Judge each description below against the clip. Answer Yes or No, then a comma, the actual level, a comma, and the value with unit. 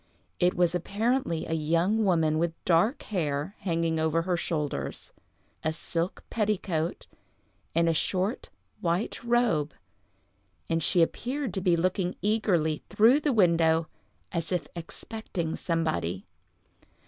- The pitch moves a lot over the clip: No, average, 4.0 semitones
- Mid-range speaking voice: Yes, medium, 170 Hz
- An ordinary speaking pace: No, slow, 125 wpm